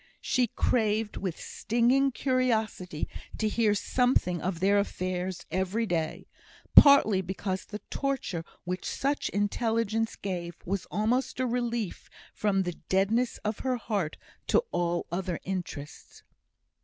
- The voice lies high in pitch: Yes, high, 205 Hz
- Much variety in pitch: No, average, 4.3 semitones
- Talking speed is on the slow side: Yes, slow, 125 wpm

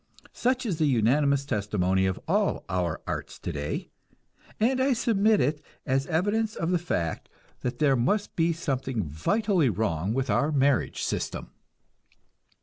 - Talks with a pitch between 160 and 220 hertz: No, medium, 140 Hz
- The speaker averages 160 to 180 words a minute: No, average, 145 wpm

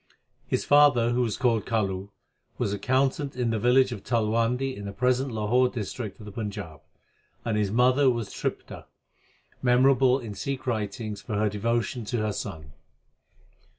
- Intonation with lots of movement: No, average, 3.4 semitones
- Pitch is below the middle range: Yes, low, 115 Hz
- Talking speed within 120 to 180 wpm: Yes, average, 155 wpm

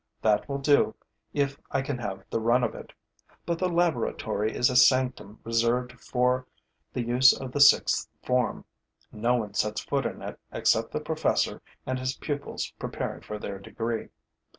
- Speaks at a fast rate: No, average, 170 wpm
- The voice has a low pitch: Yes, low, 125 Hz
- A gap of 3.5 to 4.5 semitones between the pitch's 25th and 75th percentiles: No, average, 3.0 semitones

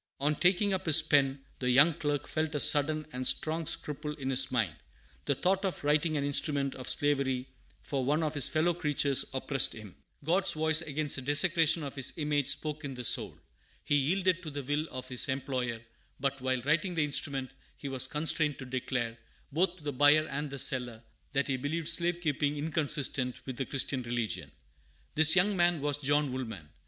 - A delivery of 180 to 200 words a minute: Yes, average, 195 wpm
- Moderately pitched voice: Yes, medium, 145 Hz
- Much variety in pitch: No, average, 3.0 semitones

